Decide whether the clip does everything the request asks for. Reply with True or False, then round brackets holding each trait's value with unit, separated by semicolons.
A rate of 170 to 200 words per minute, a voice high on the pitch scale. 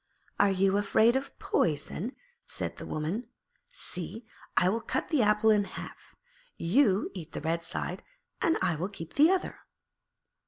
False (155 wpm; 200 Hz)